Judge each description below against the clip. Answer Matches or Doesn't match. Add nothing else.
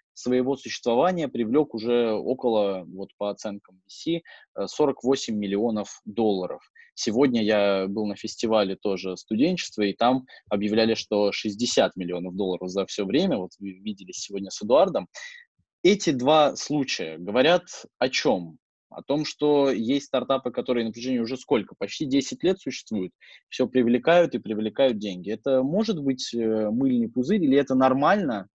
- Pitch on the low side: Matches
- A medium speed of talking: Matches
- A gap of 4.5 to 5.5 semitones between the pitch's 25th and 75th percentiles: Matches